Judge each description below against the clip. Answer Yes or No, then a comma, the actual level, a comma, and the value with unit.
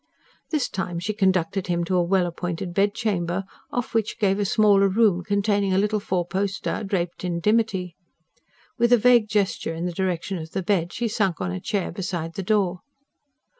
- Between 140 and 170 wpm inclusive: No, average, 185 wpm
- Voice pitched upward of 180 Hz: Yes, high, 190 Hz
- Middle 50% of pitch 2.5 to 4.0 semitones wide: Yes, average, 3.0 semitones